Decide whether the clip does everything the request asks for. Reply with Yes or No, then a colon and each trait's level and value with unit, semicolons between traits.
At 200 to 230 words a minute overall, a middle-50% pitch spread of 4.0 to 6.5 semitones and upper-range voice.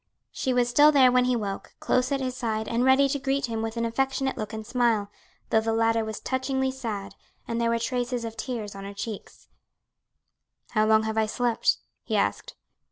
No: fast, 205 wpm; average, 2.8 semitones; high, 235 Hz